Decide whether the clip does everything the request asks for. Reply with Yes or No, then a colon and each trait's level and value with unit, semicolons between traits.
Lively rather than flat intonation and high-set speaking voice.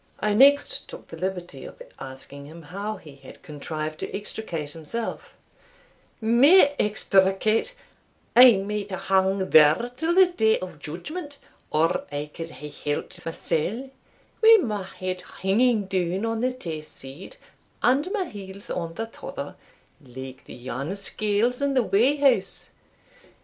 Yes: wide, 7.1 semitones; high, 195 Hz